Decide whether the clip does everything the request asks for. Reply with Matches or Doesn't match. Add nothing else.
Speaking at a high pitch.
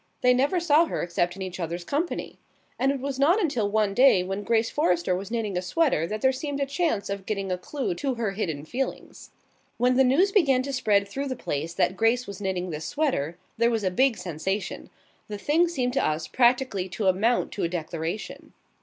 Matches